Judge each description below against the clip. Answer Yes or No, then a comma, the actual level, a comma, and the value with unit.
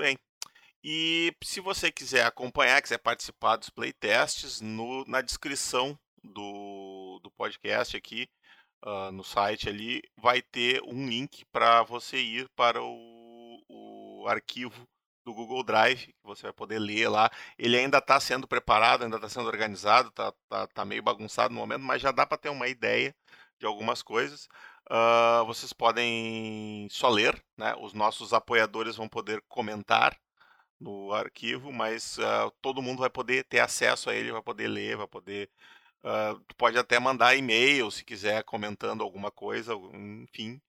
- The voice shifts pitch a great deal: No, average, 3.1 semitones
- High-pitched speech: No, low, 115 Hz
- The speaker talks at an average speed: Yes, average, 155 wpm